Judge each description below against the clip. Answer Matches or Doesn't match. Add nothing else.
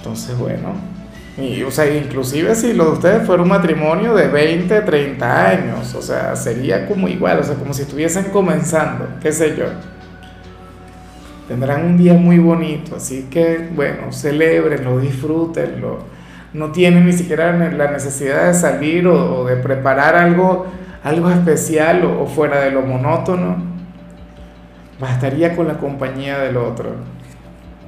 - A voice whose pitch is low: Doesn't match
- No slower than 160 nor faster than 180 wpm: Doesn't match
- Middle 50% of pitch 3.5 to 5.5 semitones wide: Matches